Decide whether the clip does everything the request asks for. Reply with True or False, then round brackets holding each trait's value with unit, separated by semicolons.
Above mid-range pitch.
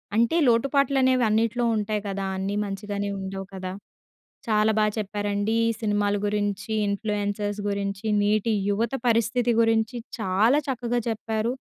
True (215 Hz)